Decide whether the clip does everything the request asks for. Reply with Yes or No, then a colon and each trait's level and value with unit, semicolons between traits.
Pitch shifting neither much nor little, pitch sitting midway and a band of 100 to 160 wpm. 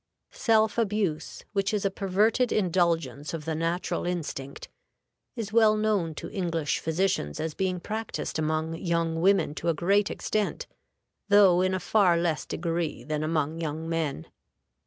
Yes: average, 3.9 semitones; medium, 175 Hz; average, 150 wpm